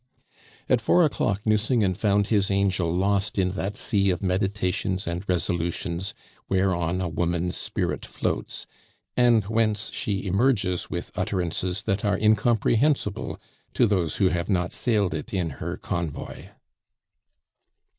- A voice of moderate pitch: No, very low, 95 Hz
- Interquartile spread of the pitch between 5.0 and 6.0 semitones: No, average, 3.0 semitones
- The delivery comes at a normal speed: No, slow, 130 wpm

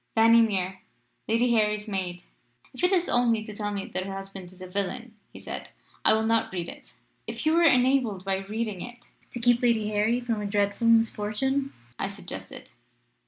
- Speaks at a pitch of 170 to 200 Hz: No, high, 220 Hz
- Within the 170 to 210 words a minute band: Yes, average, 190 wpm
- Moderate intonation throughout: Yes, average, 3.4 semitones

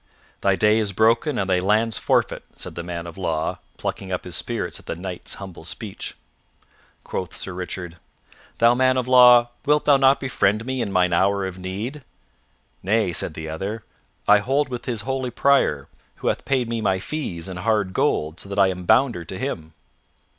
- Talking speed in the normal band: Yes, average, 190 wpm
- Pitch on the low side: Yes, low, 100 Hz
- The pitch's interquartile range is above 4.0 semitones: Yes, average, 5.2 semitones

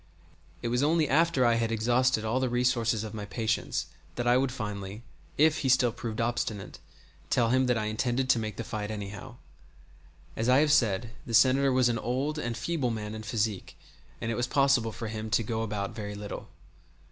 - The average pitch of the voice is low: Yes, low, 115 Hz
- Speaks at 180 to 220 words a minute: Yes, average, 200 wpm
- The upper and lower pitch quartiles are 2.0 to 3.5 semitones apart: Yes, average, 2.9 semitones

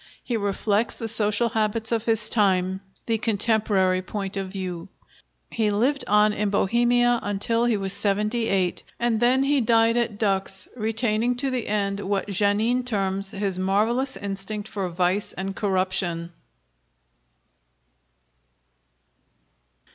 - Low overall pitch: No, high, 210 Hz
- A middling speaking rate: No, slow, 130 wpm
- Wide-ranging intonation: No, average, 2.9 semitones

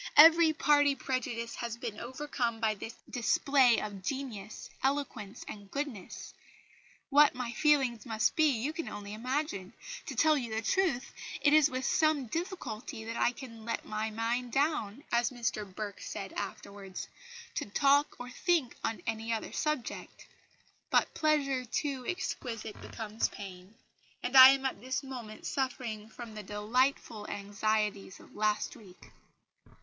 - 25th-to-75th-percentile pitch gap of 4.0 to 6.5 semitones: Yes, average, 4.4 semitones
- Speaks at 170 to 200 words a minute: No, average, 145 wpm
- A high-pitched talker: Yes, high, 240 Hz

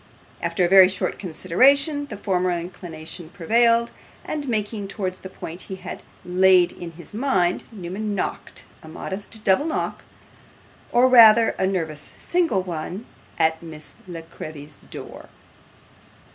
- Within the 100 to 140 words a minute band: Yes, slow, 135 wpm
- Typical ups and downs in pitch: Yes, average, 4.4 semitones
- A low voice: No, high, 190 Hz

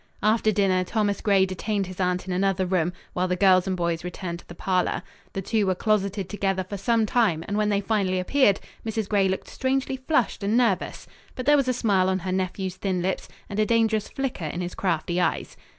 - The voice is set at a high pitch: Yes, high, 195 Hz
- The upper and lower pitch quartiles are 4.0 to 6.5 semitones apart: No, average, 2.7 semitones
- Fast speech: Yes, fast, 215 wpm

